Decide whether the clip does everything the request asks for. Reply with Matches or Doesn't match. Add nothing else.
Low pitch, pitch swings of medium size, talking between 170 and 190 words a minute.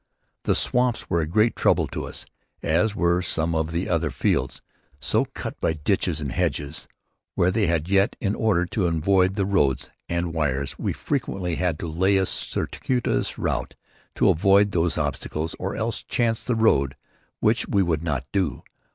Matches